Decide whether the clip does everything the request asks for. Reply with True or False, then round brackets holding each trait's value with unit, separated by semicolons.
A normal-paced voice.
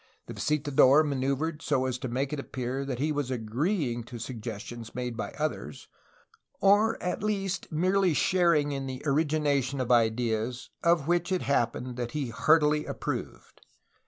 True (155 wpm)